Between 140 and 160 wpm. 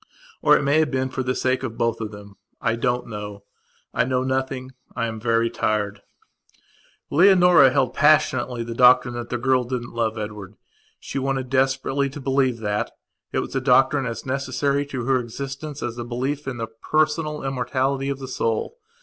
No: average, 185 wpm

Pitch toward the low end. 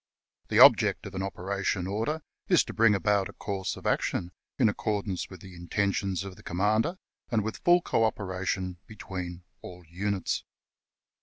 Yes: low, 100 Hz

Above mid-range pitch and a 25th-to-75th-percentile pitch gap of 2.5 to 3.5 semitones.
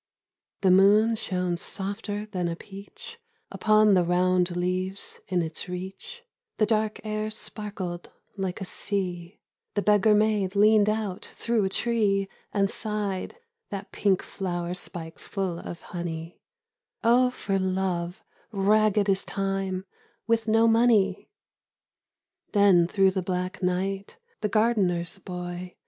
Yes: high, 195 Hz; average, 2.8 semitones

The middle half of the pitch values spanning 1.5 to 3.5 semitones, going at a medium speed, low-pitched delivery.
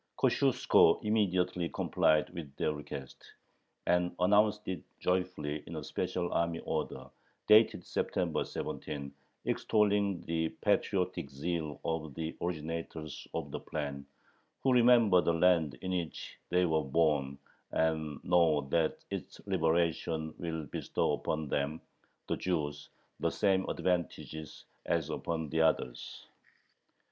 No: average, 2.9 semitones; slow, 120 wpm; very low, 80 Hz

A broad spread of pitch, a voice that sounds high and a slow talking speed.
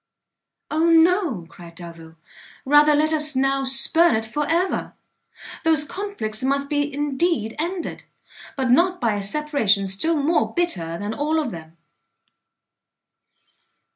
Yes: wide, 6.8 semitones; very high, 285 Hz; slow, 130 wpm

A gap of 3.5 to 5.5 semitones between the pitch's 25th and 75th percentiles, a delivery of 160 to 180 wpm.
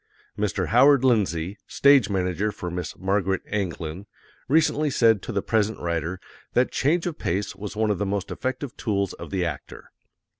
Yes: average, 4.7 semitones; average, 165 wpm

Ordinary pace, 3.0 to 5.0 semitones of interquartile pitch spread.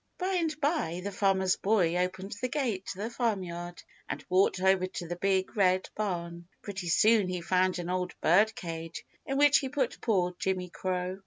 Yes: average, 180 wpm; average, 3.3 semitones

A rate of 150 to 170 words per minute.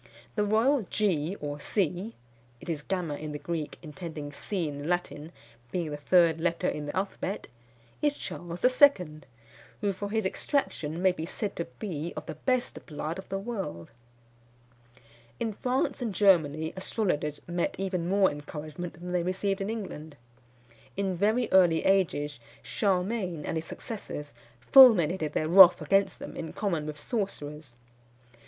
Yes: average, 155 wpm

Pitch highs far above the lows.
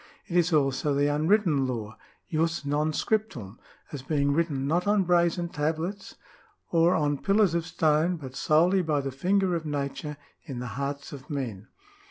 No: average, 3.7 semitones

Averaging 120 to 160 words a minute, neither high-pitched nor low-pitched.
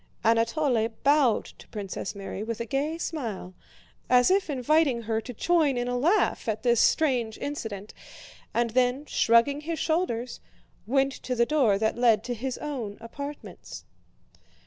No: average, 150 wpm; high, 245 Hz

